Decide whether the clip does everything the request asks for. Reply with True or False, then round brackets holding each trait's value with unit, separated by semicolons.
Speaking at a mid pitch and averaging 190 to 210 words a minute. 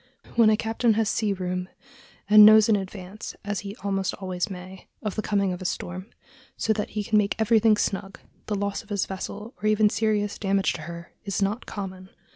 False (205 Hz; 205 wpm)